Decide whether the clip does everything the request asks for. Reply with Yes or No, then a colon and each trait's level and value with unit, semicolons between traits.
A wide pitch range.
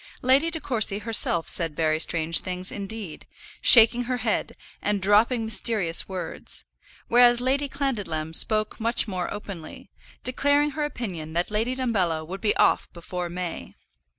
Yes: wide, 5.7 semitones